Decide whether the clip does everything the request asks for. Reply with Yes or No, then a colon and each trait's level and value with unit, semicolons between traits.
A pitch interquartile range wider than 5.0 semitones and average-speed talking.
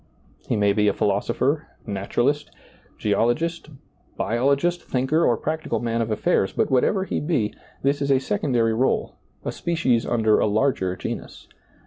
Yes: wide, 5.4 semitones; average, 145 wpm